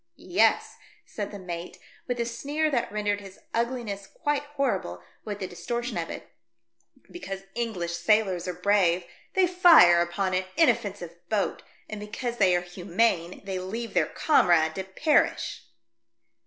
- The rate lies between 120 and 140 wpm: No, average, 150 wpm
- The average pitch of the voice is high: Yes, high, 200 Hz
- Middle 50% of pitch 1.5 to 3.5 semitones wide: No, average, 4.9 semitones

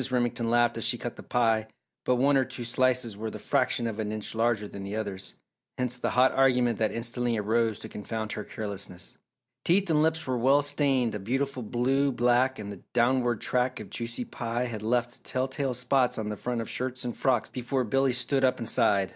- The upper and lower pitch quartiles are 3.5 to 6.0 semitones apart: No, narrow, 2.6 semitones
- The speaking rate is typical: No, fast, 210 wpm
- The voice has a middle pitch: No, low, 120 Hz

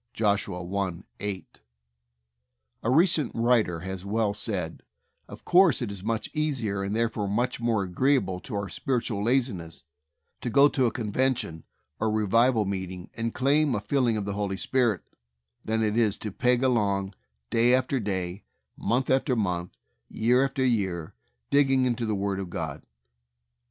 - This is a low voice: Yes, low, 110 Hz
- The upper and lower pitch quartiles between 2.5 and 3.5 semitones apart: No, average, 4.3 semitones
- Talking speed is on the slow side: No, average, 155 wpm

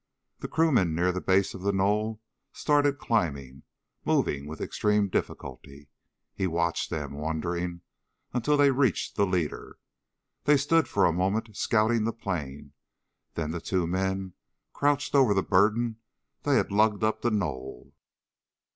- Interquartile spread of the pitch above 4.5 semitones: Yes, average, 5.0 semitones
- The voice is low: Yes, very low, 95 Hz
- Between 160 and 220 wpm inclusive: No, average, 145 wpm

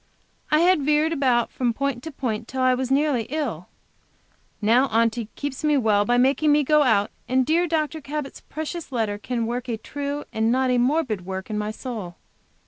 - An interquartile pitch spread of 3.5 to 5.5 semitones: Yes, average, 4.6 semitones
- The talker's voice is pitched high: Yes, very high, 255 Hz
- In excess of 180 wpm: Yes, average, 195 wpm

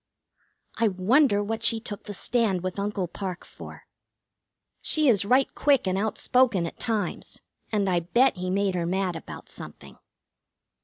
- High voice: Yes, high, 200 Hz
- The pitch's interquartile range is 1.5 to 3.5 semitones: No, average, 3.9 semitones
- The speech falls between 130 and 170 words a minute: Yes, average, 155 wpm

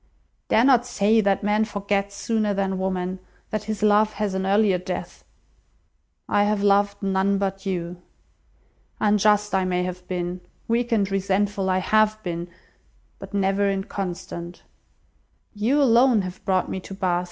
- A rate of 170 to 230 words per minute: No, average, 150 wpm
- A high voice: Yes, high, 200 Hz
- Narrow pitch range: Yes, narrow, 2.0 semitones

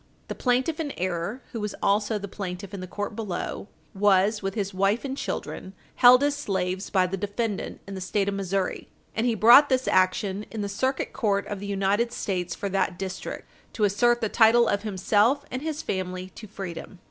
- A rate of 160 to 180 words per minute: No, average, 200 wpm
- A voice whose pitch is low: No, high, 205 Hz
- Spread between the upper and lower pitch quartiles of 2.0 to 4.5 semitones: Yes, average, 3.4 semitones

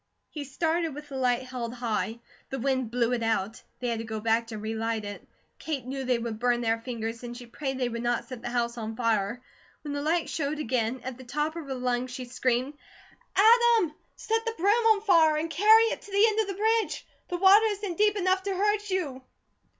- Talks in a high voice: Yes, very high, 260 Hz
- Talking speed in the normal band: No, fast, 225 wpm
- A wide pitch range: Yes, wide, 7.8 semitones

